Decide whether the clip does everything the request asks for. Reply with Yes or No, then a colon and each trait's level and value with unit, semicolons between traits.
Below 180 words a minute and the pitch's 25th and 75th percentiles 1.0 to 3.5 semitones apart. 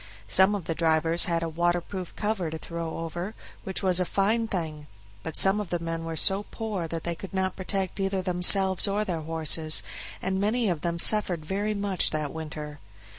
No: average, 195 wpm; average, 3.0 semitones